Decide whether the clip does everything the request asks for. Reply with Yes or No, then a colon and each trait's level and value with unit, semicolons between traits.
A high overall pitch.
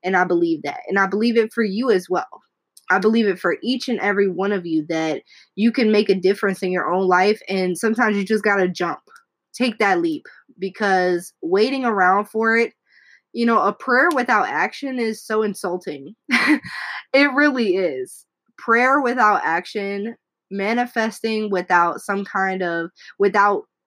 Yes: high, 205 Hz